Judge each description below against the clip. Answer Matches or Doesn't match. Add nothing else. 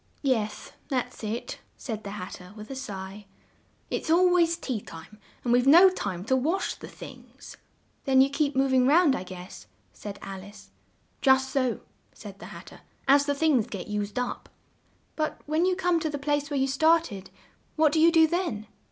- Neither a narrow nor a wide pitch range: Doesn't match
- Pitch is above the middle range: Matches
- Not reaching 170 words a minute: Doesn't match